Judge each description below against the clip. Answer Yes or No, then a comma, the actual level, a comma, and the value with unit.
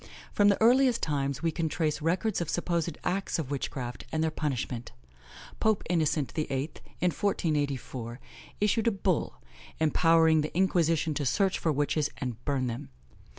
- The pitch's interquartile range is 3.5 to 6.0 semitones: Yes, average, 4.1 semitones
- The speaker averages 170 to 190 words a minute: No, average, 150 wpm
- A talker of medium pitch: Yes, medium, 160 Hz